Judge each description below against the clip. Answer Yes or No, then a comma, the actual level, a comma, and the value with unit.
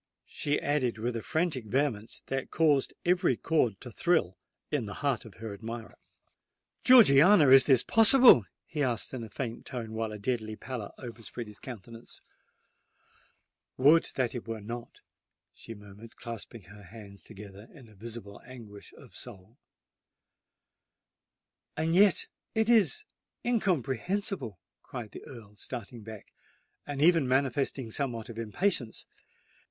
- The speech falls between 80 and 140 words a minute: Yes, slow, 135 wpm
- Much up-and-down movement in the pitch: No, average, 4.7 semitones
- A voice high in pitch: No, low, 120 Hz